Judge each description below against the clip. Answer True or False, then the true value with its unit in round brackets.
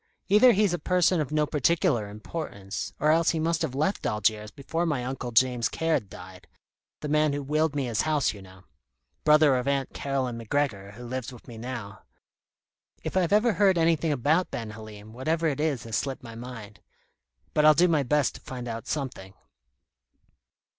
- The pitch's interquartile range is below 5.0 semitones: False (5.6 semitones)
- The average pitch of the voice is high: False (135 Hz)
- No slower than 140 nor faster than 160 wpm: False (185 wpm)